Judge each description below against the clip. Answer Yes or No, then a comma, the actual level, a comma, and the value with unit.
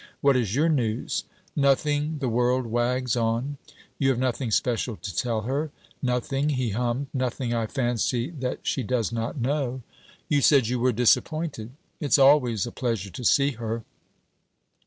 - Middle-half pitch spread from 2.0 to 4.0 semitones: Yes, average, 2.9 semitones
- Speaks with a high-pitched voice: No, low, 125 Hz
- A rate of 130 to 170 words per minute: Yes, average, 155 wpm